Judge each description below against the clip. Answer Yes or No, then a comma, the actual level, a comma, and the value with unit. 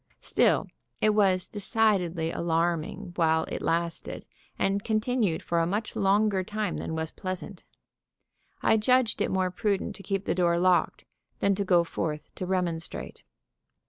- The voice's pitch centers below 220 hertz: Yes, medium, 185 Hz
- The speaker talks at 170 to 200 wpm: No, average, 145 wpm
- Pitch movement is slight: No, average, 3.4 semitones